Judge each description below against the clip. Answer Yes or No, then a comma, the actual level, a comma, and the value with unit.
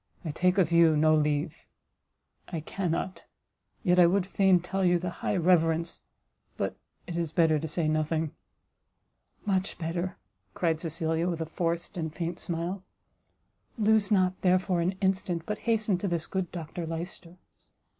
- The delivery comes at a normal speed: Yes, average, 155 wpm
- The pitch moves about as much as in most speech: No, narrow, 2.3 semitones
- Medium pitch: Yes, medium, 175 Hz